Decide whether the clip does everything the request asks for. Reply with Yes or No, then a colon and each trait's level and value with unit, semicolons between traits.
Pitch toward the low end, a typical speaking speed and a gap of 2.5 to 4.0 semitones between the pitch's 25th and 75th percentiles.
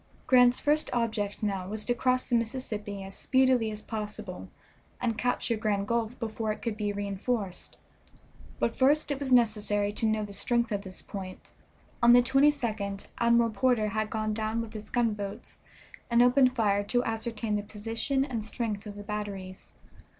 No: high, 220 Hz; average, 170 wpm; average, 2.8 semitones